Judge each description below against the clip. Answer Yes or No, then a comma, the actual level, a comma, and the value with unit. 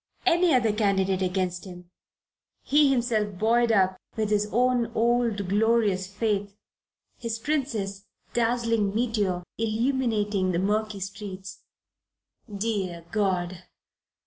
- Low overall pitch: No, high, 210 Hz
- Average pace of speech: No, slow, 105 wpm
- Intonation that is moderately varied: Yes, average, 3.3 semitones